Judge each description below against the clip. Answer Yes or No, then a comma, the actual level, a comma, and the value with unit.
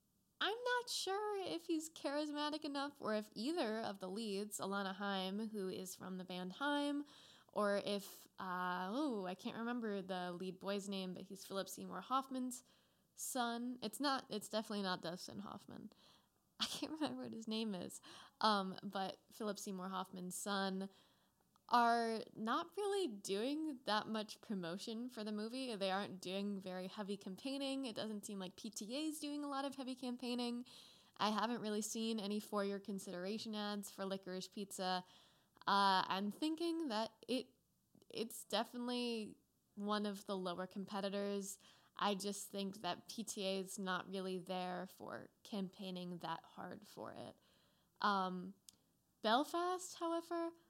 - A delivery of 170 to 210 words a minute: No, average, 150 wpm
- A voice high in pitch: Yes, high, 210 Hz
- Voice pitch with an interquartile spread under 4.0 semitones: No, average, 4.4 semitones